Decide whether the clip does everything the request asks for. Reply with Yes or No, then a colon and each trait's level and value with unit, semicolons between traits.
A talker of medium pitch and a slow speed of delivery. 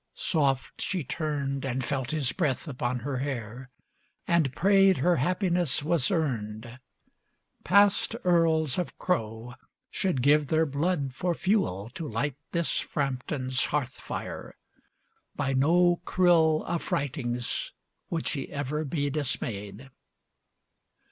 Yes: medium, 145 Hz; slow, 115 wpm